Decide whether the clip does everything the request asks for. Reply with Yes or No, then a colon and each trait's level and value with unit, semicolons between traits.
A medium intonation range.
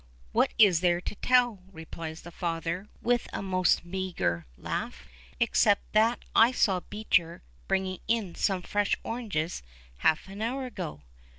Yes: average, 4.3 semitones